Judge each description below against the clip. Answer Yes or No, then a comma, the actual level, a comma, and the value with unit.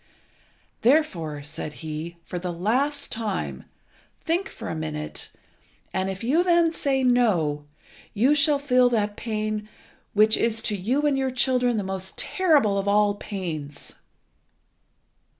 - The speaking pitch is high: Yes, high, 215 Hz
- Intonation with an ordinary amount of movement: No, wide, 6.3 semitones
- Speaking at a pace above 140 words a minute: No, slow, 135 wpm